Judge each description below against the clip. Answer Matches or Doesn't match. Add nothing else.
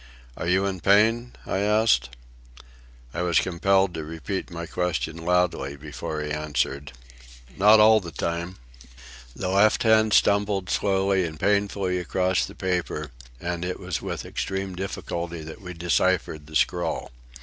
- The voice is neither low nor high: Doesn't match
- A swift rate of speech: Doesn't match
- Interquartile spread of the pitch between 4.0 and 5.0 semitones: Doesn't match